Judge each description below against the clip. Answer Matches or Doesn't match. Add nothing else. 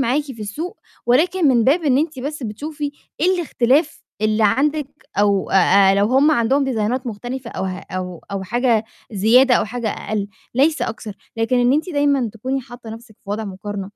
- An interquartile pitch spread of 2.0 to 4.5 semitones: Doesn't match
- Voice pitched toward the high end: Matches